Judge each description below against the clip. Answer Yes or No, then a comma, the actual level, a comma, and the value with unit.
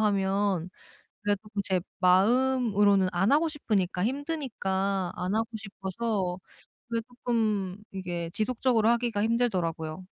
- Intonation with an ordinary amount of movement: Yes, average, 3.7 semitones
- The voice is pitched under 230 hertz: Yes, high, 205 Hz